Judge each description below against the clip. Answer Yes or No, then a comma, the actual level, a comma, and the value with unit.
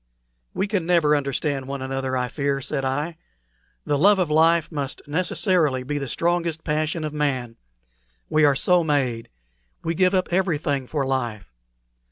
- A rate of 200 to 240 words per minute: No, average, 160 wpm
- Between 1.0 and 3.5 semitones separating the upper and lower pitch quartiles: No, average, 3.9 semitones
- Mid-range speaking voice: Yes, medium, 150 Hz